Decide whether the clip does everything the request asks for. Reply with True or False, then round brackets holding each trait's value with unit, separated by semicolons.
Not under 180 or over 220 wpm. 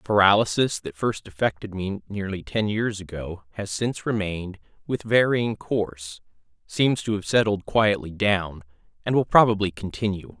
False (145 wpm)